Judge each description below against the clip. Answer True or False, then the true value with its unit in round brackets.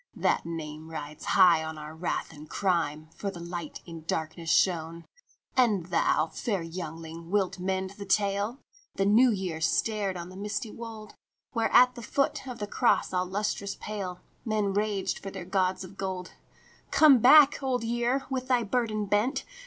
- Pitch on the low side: False (195 Hz)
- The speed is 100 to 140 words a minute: False (175 wpm)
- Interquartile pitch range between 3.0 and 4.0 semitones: False (4.6 semitones)